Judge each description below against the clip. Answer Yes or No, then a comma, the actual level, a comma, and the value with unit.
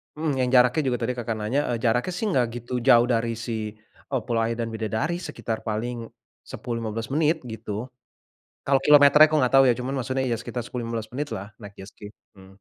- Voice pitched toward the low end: Yes, low, 120 Hz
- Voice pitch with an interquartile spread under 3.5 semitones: Yes, average, 2.9 semitones